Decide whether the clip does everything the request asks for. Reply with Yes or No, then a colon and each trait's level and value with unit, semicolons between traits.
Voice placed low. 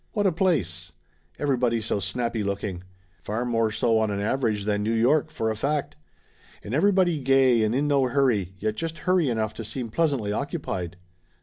Yes: low, 115 Hz